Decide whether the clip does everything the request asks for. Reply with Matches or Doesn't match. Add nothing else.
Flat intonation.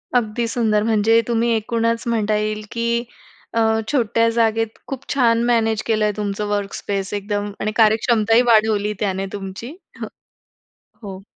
Matches